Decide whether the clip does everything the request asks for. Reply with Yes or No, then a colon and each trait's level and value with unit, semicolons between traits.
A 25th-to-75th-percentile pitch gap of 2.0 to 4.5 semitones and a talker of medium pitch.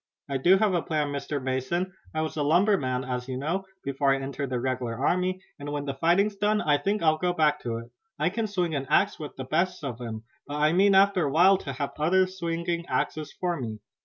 No: average, 5.3 semitones; medium, 155 Hz